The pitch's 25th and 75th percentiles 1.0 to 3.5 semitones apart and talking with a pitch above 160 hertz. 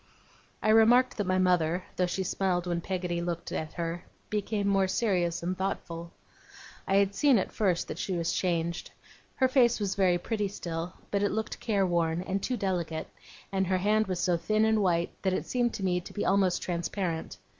Yes: average, 2.9 semitones; medium, 185 Hz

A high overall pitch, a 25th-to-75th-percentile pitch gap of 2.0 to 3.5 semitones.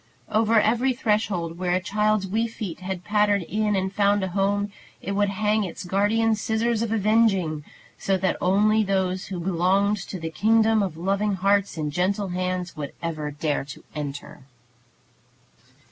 Yes: high, 195 Hz; average, 2.9 semitones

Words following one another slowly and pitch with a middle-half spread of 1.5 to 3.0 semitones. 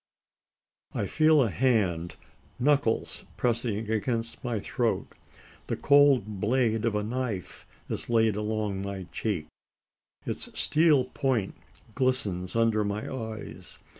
No: slow, 115 wpm; average, 3.6 semitones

